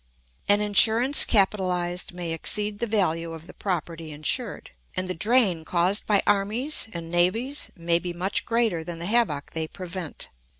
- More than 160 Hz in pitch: Yes, medium, 185 Hz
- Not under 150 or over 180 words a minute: Yes, average, 160 wpm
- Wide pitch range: No, average, 3.9 semitones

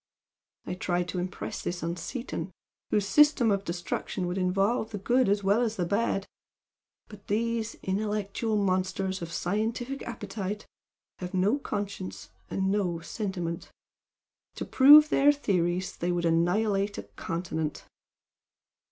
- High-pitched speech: Yes, high, 195 Hz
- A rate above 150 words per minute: No, slow, 135 wpm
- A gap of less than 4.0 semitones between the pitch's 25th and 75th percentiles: Yes, average, 3.6 semitones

